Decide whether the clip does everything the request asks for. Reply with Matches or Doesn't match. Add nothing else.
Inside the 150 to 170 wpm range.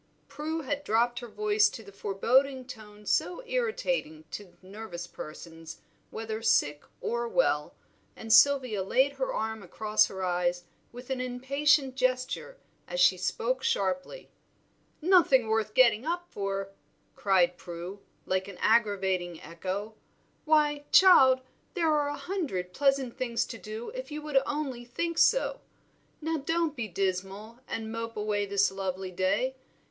Doesn't match